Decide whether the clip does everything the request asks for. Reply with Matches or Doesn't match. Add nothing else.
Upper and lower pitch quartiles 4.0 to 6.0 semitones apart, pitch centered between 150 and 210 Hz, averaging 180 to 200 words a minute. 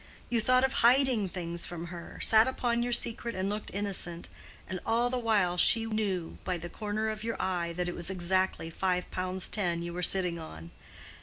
Matches